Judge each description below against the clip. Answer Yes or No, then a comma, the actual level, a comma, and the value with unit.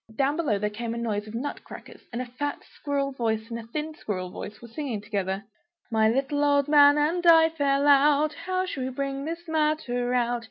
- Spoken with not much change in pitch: No, average, 4.5 semitones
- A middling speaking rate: No, fast, 210 wpm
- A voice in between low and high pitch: No, very high, 275 Hz